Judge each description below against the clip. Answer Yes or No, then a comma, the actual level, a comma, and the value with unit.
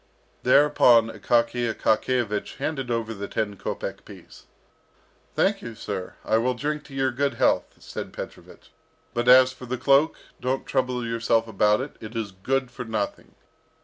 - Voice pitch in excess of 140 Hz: No, low, 120 Hz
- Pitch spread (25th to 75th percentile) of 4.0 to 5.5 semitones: No, average, 2.7 semitones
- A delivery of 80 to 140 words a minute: No, average, 150 wpm